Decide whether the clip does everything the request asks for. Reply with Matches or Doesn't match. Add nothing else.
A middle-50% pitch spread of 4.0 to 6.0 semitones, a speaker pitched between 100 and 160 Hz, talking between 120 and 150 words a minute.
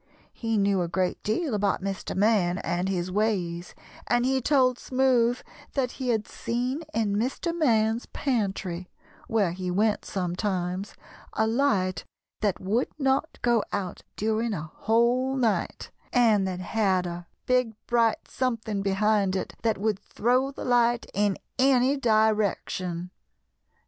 Doesn't match